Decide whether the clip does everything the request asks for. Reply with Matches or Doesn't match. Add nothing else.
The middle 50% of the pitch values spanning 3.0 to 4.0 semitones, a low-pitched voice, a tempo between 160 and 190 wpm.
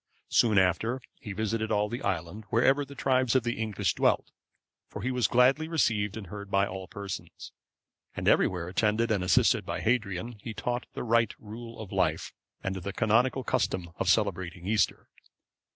Matches